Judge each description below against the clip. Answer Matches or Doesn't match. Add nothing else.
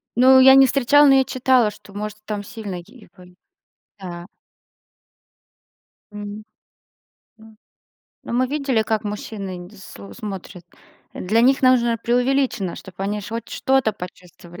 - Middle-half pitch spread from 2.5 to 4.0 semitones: Doesn't match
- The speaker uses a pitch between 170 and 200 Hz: Doesn't match